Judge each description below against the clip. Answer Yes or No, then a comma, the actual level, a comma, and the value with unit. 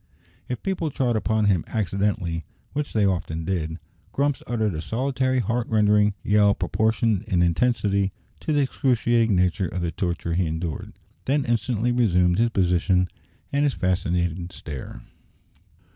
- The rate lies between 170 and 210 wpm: No, average, 145 wpm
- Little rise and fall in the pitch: No, average, 5.2 semitones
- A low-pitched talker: Yes, low, 105 Hz